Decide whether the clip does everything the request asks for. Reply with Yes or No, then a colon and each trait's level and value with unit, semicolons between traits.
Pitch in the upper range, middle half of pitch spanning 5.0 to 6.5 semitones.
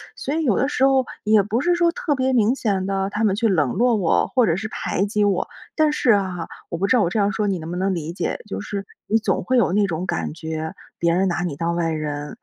Yes: high, 195 Hz; average, 5.3 semitones